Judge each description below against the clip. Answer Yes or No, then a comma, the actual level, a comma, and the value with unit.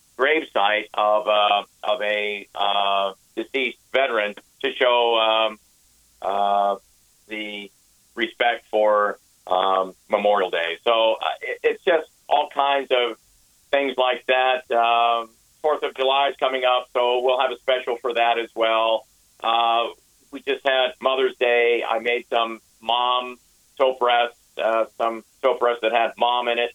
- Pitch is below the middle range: Yes, low, 115 Hz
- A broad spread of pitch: No, average, 3.2 semitones